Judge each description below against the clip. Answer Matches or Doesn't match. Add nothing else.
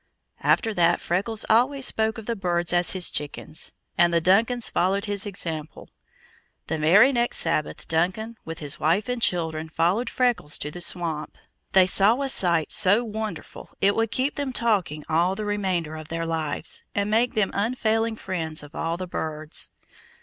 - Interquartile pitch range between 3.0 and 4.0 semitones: Doesn't match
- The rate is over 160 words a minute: Matches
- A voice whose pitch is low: Doesn't match